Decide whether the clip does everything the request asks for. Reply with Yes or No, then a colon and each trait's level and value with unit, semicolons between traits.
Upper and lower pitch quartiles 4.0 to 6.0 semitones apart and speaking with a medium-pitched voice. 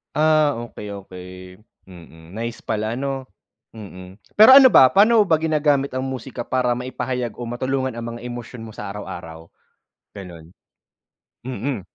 No: average, 4.6 semitones; low, 120 Hz